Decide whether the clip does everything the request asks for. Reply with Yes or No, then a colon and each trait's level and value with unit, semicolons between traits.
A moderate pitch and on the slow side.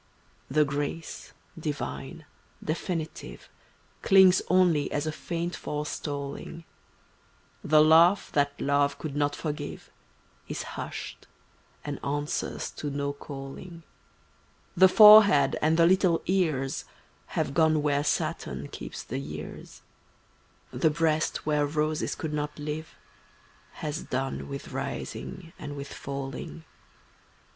Yes: medium, 150 Hz; slow, 110 wpm